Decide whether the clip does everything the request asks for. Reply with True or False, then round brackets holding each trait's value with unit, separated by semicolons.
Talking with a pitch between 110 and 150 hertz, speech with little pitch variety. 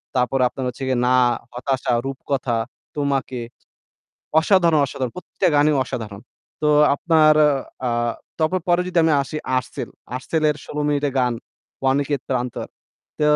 False (140 Hz; 3.3 semitones)